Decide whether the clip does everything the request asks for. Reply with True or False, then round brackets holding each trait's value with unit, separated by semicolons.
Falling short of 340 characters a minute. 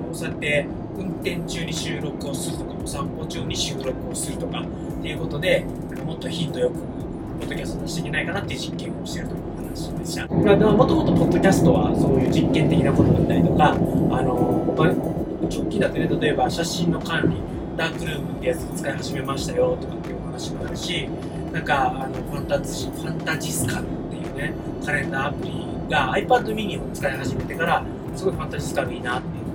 False (440 characters per minute)